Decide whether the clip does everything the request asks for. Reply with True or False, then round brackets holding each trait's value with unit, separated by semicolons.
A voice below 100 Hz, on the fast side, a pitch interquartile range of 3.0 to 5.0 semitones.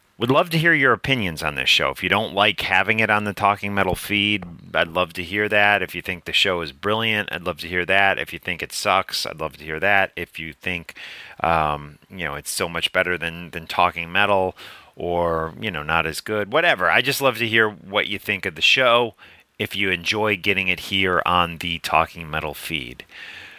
True (90 Hz; 230 wpm; 3.6 semitones)